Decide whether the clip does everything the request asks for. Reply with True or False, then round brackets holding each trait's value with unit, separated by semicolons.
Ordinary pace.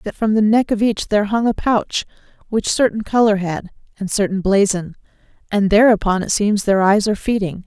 True (195 wpm)